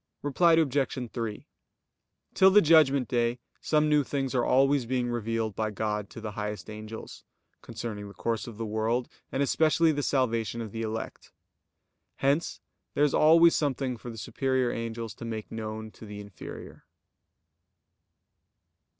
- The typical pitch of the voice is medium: No, low, 120 Hz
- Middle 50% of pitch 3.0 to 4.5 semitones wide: Yes, average, 4.1 semitones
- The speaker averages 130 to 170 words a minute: Yes, average, 150 wpm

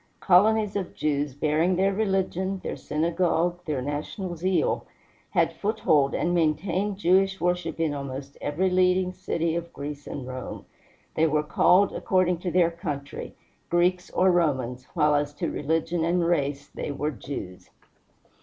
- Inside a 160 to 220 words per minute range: No, average, 145 wpm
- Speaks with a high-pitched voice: No, medium, 170 Hz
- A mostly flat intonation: No, average, 3.9 semitones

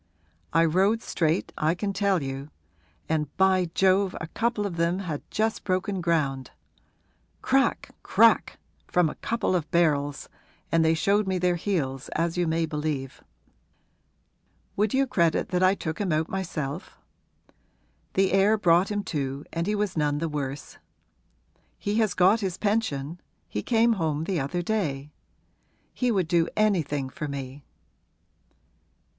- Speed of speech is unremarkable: Yes, average, 150 wpm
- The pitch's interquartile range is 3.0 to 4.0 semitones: No, average, 4.6 semitones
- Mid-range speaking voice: Yes, medium, 175 Hz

